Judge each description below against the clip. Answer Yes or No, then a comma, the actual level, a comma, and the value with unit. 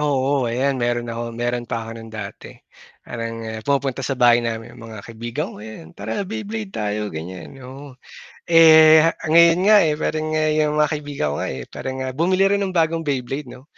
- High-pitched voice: No, low, 130 Hz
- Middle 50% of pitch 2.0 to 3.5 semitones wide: No, average, 5.3 semitones